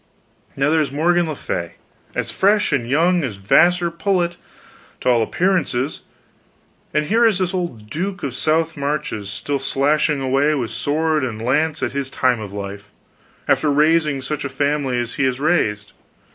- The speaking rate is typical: Yes, average, 175 wpm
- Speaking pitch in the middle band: Yes, medium, 145 Hz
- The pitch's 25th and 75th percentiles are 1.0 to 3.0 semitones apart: No, average, 4.6 semitones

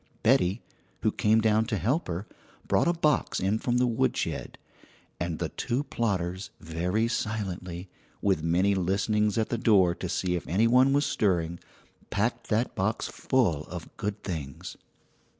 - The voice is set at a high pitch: No, low, 100 Hz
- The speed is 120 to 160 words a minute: Yes, average, 155 wpm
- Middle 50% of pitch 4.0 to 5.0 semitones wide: Yes, average, 4.5 semitones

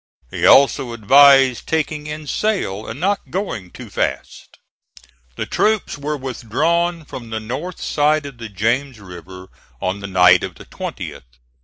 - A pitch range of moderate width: No, wide, 6.3 semitones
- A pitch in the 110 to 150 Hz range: Yes, low, 135 Hz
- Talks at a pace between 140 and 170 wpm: Yes, average, 150 wpm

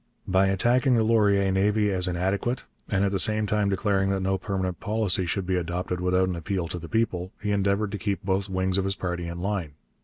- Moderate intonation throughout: No, narrow, 1.9 semitones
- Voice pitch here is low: Yes, very low, 95 Hz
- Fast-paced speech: Yes, fast, 220 wpm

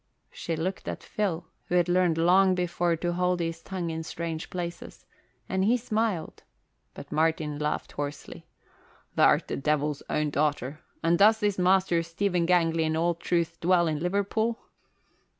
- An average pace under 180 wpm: Yes, average, 160 wpm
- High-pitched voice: No, medium, 170 Hz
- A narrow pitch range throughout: Yes, narrow, 2.3 semitones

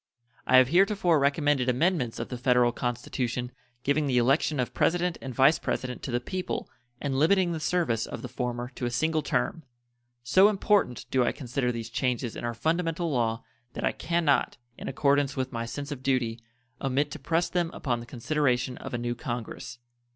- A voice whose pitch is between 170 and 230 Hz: No, low, 130 Hz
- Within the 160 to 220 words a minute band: Yes, average, 190 wpm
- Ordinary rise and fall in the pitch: Yes, average, 4.4 semitones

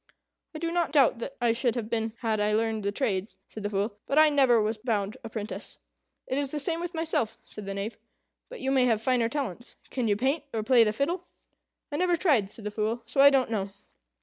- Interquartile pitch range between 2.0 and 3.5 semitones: No, average, 4.6 semitones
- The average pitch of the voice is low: No, high, 235 Hz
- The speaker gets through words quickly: Yes, fast, 230 wpm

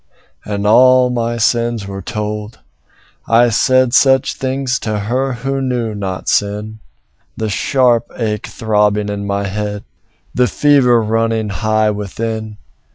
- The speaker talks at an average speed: No, slow, 130 wpm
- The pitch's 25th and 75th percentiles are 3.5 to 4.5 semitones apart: No, average, 2.9 semitones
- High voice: No, low, 110 Hz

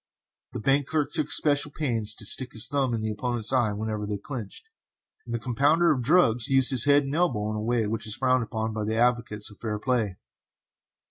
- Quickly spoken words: Yes, fast, 210 wpm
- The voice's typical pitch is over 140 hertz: No, low, 120 Hz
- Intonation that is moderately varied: Yes, average, 4.1 semitones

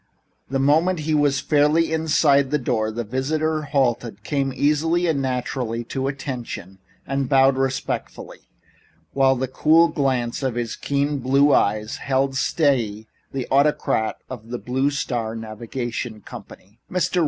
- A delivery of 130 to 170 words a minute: Yes, average, 140 wpm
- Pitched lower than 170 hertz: Yes, low, 135 Hz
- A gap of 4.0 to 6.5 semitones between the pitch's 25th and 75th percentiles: No, average, 3.5 semitones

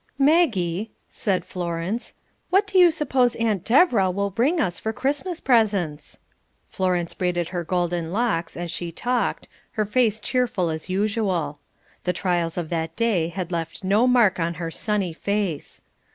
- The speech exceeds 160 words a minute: No, average, 150 wpm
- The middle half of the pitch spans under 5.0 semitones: No, average, 5.3 semitones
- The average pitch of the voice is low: No, high, 190 Hz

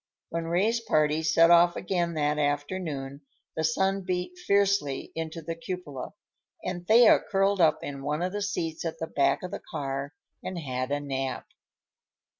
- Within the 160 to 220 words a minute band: Yes, average, 165 wpm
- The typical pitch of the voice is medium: Yes, medium, 165 Hz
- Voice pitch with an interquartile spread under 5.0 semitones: Yes, average, 4.0 semitones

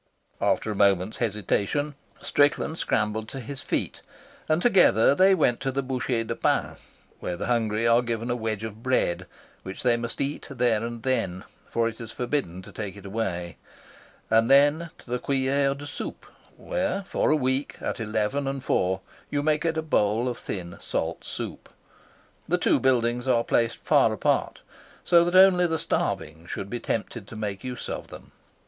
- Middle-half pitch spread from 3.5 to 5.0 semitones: Yes, average, 4.6 semitones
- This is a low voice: Yes, low, 120 Hz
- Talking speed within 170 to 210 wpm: Yes, average, 180 wpm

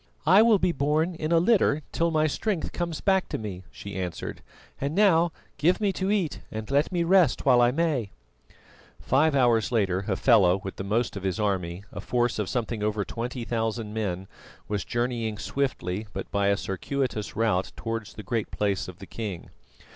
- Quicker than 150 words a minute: Yes, average, 185 wpm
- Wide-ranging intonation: Yes, wide, 7.4 semitones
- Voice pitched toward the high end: No, low, 120 Hz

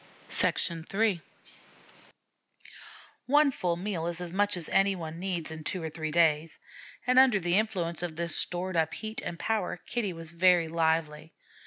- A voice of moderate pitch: Yes, medium, 175 Hz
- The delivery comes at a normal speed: Yes, average, 160 wpm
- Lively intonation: No, average, 3.1 semitones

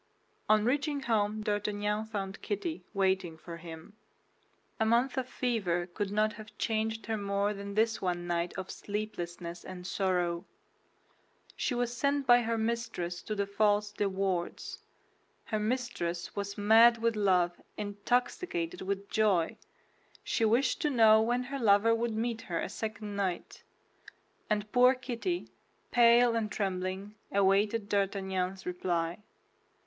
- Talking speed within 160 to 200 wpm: No, average, 140 wpm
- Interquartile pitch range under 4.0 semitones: Yes, average, 3.3 semitones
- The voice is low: No, high, 210 Hz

